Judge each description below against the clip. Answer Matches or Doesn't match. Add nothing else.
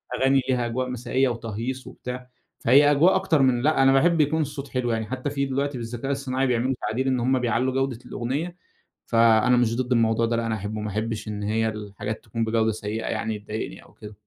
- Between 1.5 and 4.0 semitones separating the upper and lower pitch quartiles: Matches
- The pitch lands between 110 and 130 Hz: Matches